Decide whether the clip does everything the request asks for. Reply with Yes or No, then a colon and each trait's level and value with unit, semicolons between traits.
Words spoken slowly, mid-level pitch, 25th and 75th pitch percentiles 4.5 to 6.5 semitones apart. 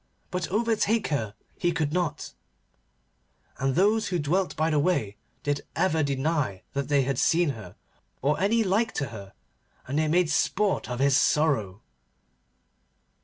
No: average, 150 wpm; medium, 155 Hz; average, 5.1 semitones